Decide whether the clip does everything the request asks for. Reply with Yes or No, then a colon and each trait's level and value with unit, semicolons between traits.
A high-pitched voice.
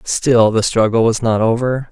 No: low, 115 Hz